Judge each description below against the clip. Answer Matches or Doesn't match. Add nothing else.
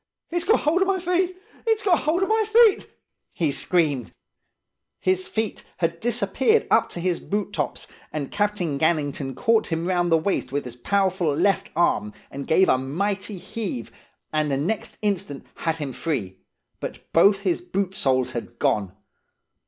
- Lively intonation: Matches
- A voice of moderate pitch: Matches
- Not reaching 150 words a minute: Doesn't match